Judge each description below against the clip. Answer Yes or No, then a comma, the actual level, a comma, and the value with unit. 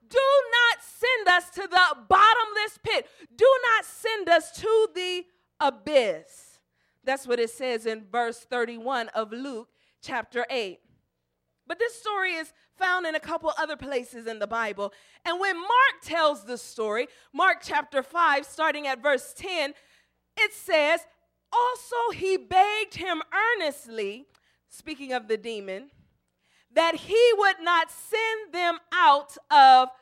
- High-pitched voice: Yes, very high, 325 Hz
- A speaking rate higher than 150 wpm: No, average, 140 wpm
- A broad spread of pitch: Yes, wide, 6.7 semitones